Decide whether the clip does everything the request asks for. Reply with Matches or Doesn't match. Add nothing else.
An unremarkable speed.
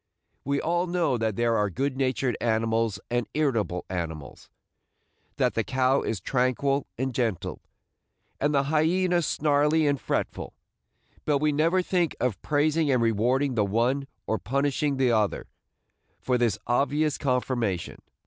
Matches